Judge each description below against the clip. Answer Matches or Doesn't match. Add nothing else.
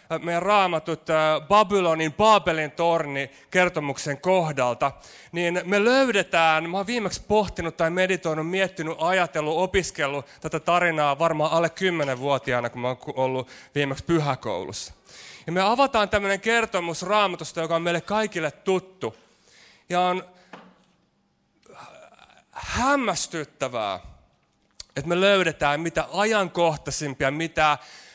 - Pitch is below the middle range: Doesn't match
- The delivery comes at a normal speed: Matches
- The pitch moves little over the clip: Doesn't match